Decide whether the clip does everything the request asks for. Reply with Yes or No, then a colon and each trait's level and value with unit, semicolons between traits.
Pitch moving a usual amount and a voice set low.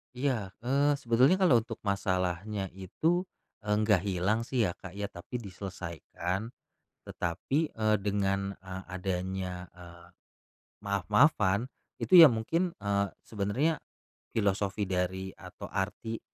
Yes: average, 3.6 semitones; low, 100 Hz